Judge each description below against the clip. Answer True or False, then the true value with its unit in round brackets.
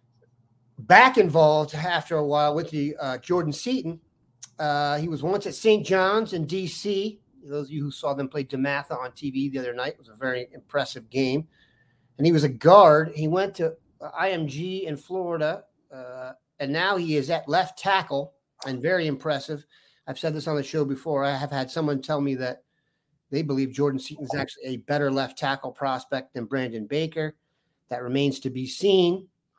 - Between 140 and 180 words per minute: False (190 wpm)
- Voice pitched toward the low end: False (145 Hz)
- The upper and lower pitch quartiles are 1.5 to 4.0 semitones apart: True (3.3 semitones)